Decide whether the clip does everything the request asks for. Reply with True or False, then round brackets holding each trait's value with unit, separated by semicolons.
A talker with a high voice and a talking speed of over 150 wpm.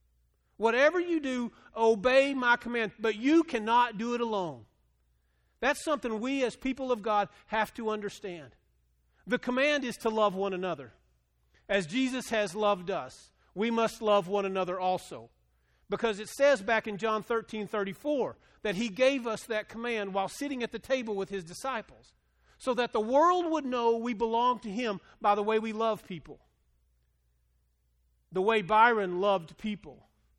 True (215 Hz; 160 wpm)